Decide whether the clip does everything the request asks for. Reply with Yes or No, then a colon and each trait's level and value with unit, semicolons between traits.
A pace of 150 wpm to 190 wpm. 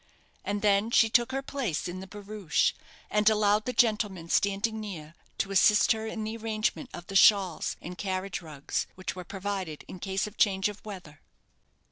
Yes: average, 175 wpm